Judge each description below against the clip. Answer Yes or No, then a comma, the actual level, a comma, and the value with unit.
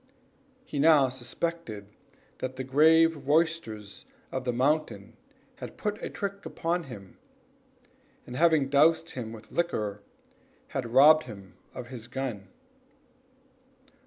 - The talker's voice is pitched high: No, low, 135 Hz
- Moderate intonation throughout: No, wide, 5.9 semitones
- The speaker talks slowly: Yes, slow, 120 wpm